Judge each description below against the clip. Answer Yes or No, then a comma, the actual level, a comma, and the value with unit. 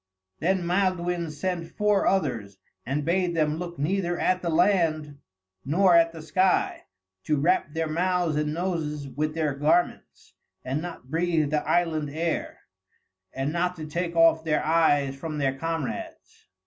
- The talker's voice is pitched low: No, medium, 165 Hz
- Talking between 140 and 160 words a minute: Yes, average, 150 wpm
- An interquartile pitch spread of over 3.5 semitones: No, average, 2.7 semitones